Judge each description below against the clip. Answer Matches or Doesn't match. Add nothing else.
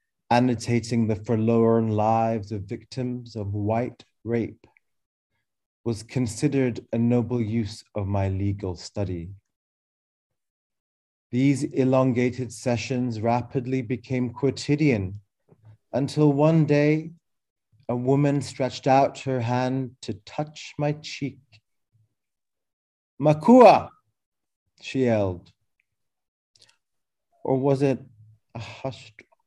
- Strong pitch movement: Doesn't match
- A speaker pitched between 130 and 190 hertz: Doesn't match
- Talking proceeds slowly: Matches